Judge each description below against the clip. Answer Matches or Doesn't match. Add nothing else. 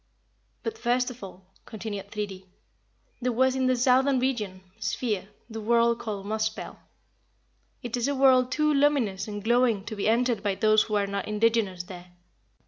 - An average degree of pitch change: Matches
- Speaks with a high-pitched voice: Matches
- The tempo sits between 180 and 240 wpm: Doesn't match